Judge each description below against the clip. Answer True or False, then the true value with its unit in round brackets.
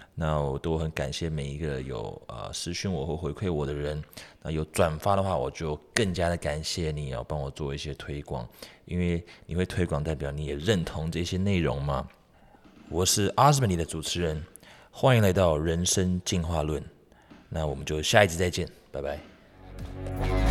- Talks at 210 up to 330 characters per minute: True (265 characters per minute)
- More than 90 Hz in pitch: False (80 Hz)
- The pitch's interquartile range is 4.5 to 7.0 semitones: False (3.7 semitones)